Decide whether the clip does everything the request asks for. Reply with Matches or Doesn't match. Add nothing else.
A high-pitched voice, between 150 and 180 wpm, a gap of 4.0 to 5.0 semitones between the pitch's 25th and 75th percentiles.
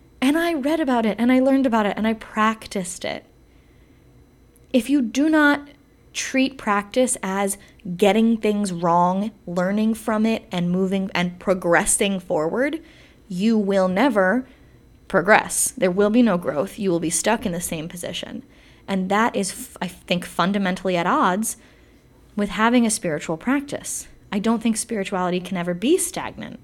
Matches